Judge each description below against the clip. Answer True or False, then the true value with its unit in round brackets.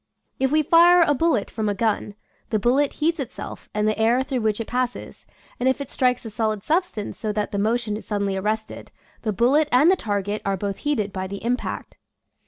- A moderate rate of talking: False (210 wpm)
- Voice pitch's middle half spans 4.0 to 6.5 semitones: True (4.3 semitones)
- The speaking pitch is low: False (230 Hz)